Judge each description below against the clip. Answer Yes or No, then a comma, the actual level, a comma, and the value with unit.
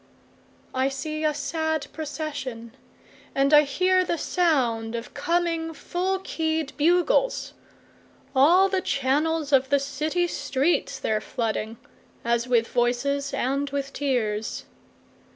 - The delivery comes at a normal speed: No, slow, 105 wpm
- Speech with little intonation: No, average, 3.9 semitones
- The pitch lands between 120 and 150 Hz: No, very high, 285 Hz